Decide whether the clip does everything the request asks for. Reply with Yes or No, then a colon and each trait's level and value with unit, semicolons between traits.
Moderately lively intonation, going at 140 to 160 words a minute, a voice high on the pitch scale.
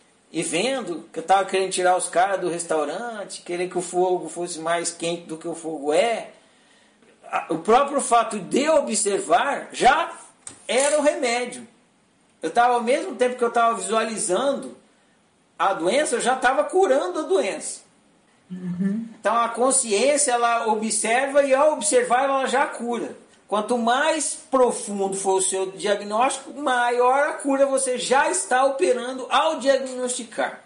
No: wide, 5.8 semitones; average, 155 wpm; high, 235 Hz